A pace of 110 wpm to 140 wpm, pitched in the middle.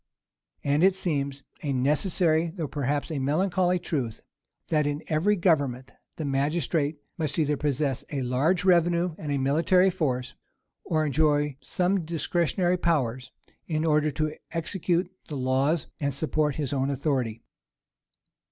Yes: slow, 135 wpm; medium, 150 Hz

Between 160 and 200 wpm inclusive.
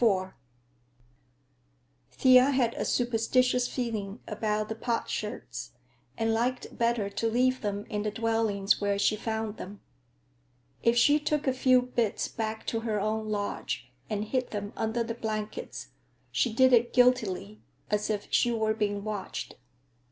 No: average, 145 wpm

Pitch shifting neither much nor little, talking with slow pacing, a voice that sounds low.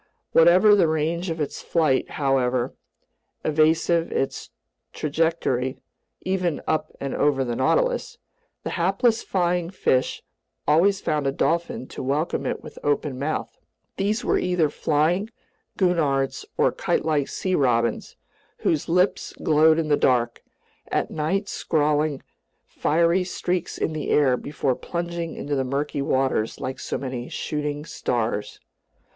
No: average, 3.9 semitones; slow, 130 wpm; medium, 155 Hz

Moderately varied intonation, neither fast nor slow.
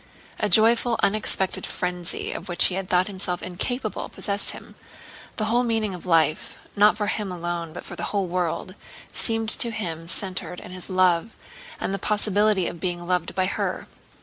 Yes: average, 3.0 semitones; average, 170 wpm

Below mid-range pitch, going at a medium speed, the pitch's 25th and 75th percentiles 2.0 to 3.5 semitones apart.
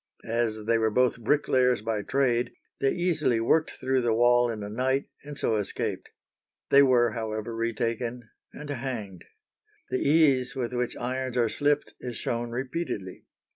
Yes: low, 120 Hz; average, 155 wpm; narrow, 2.6 semitones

